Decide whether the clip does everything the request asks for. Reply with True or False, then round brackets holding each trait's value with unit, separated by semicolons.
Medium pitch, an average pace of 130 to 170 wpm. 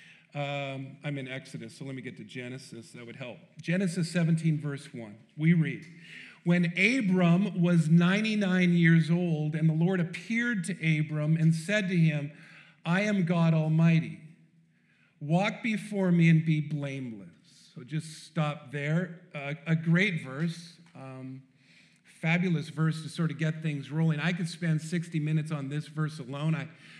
True (160 Hz; 160 wpm)